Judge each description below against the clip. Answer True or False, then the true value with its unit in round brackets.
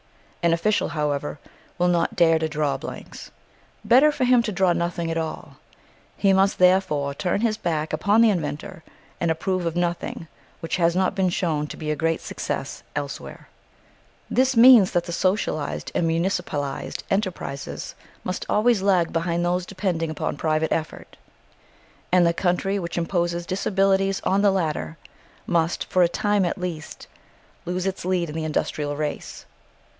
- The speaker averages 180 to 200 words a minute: False (160 wpm)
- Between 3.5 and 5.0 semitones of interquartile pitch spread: False (3.0 semitones)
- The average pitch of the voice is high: False (175 Hz)